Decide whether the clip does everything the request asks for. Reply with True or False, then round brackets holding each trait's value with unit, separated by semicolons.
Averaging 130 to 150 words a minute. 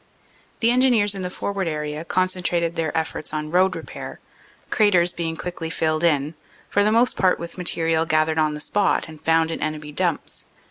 False (180 wpm)